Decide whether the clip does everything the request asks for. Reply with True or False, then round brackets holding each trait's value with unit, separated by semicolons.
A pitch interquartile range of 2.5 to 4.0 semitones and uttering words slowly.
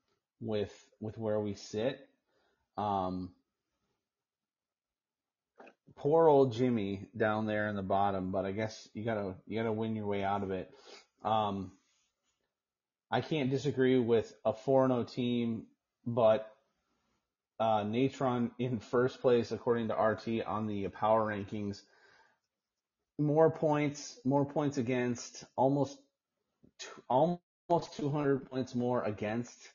True (3.7 semitones; 120 wpm)